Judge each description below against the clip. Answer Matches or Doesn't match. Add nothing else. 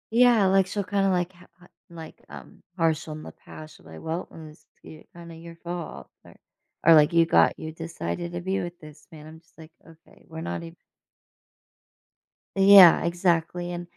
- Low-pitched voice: Doesn't match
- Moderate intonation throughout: Doesn't match